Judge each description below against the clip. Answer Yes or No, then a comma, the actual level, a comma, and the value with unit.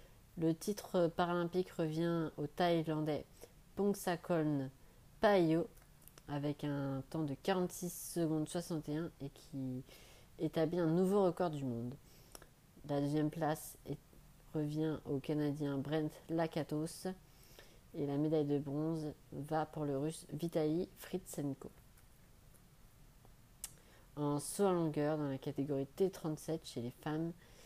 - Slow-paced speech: Yes, slow, 115 wpm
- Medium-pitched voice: Yes, medium, 155 Hz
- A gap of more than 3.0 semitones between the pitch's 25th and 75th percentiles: No, average, 2.7 semitones